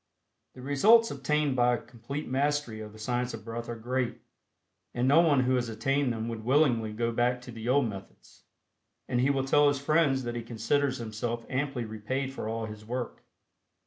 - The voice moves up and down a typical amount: Yes, average, 3.3 semitones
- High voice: No, low, 125 Hz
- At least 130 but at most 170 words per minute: No, average, 195 wpm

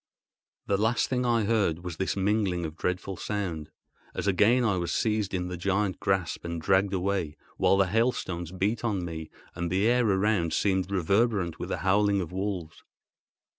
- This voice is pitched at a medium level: No, very low, 95 Hz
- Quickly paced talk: No, average, 175 wpm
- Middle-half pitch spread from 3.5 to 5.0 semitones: No, average, 3.0 semitones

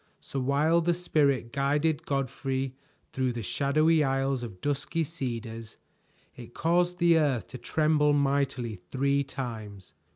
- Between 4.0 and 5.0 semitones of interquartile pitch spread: No, average, 3.5 semitones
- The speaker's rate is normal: No, slow, 130 wpm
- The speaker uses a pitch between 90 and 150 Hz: Yes, medium, 140 Hz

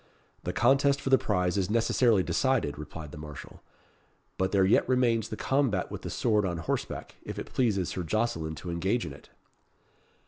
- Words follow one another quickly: No, average, 180 wpm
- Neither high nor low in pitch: No, low, 100 Hz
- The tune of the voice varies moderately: No, wide, 5.8 semitones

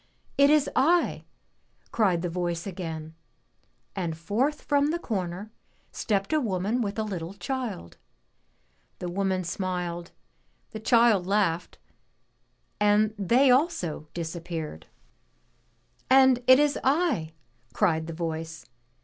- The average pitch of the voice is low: No, high, 195 Hz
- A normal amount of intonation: No, wide, 6.6 semitones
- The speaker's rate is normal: No, slow, 115 wpm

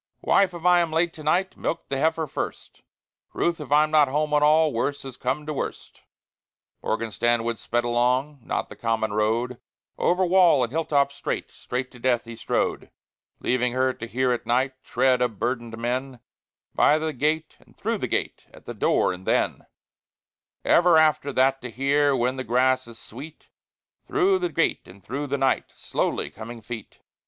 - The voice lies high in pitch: No, low, 130 Hz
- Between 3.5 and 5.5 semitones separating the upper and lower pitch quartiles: Yes, average, 4.3 semitones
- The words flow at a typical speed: Yes, average, 185 wpm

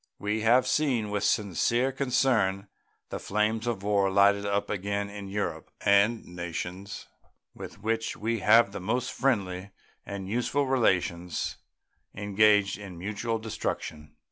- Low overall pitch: Yes, low, 105 Hz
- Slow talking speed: Yes, slow, 130 wpm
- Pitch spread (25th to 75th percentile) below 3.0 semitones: Yes, narrow, 2.5 semitones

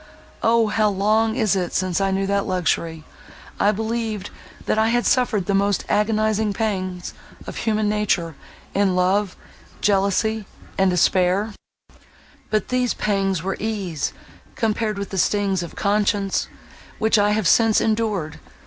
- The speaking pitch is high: Yes, high, 205 Hz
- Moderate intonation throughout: No, narrow, 2.3 semitones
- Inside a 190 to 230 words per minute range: No, average, 140 wpm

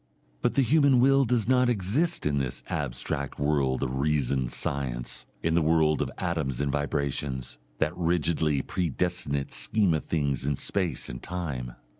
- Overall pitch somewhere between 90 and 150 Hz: No, very low, 75 Hz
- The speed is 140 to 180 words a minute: Yes, average, 155 wpm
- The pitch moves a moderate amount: Yes, average, 4.7 semitones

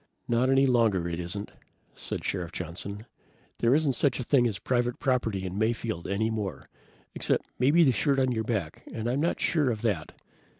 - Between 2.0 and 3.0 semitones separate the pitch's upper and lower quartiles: No, average, 4.6 semitones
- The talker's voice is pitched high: No, low, 115 Hz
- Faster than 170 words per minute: Yes, average, 185 wpm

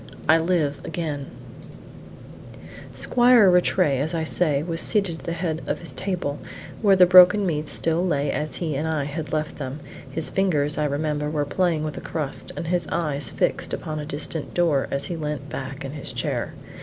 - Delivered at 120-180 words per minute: No, average, 190 wpm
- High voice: No, medium, 155 Hz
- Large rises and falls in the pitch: No, average, 3.1 semitones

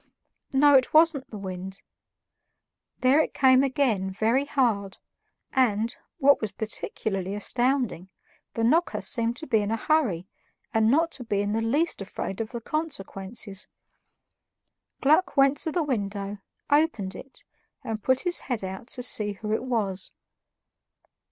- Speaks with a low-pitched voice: No, high, 230 Hz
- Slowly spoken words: No, average, 145 wpm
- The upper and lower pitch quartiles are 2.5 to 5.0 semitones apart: No, wide, 5.4 semitones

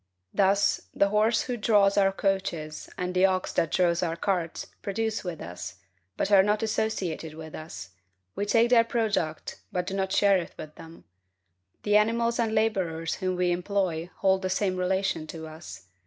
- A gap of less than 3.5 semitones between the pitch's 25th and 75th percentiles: No, average, 3.8 semitones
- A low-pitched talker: No, high, 190 Hz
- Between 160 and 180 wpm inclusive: Yes, average, 175 wpm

